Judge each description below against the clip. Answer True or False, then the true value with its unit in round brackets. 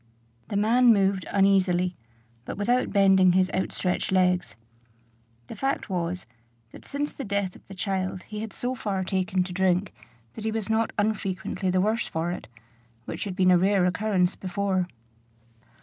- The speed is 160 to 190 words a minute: True (165 wpm)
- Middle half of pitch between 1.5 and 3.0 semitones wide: True (2.4 semitones)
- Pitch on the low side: False (190 Hz)